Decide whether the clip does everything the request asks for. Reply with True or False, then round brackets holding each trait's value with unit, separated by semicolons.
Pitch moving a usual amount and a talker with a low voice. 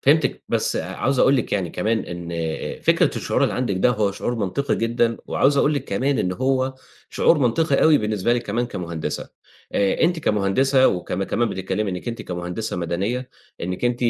False (5.7 semitones; 115 Hz)